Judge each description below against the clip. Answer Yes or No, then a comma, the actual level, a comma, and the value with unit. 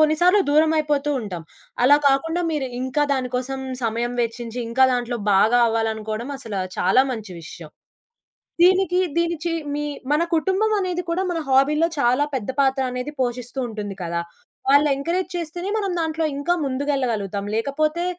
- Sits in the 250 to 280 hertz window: Yes, very high, 270 Hz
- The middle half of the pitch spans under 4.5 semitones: No, wide, 5.4 semitones